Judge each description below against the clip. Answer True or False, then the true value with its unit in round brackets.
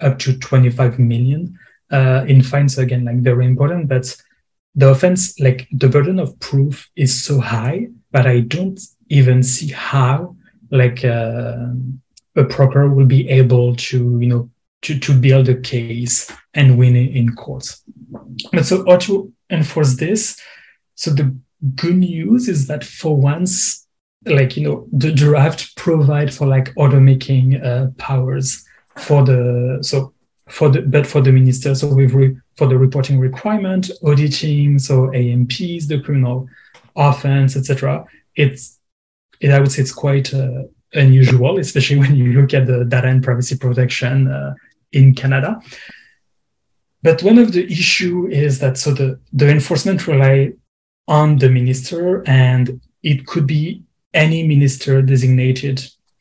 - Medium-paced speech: True (150 wpm)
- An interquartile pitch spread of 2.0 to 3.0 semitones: True (2.5 semitones)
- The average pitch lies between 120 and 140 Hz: True (135 Hz)